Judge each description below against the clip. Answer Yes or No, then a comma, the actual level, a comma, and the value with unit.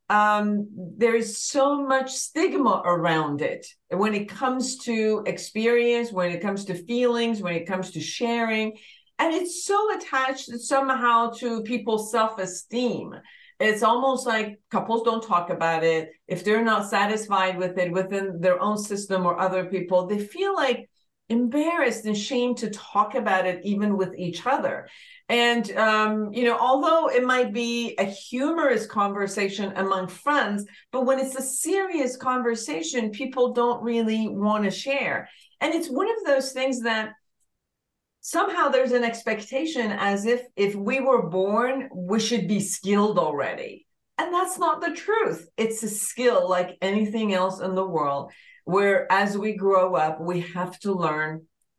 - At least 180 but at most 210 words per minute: No, average, 160 wpm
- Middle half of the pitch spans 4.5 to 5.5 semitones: Yes, average, 5.0 semitones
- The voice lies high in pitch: Yes, high, 220 Hz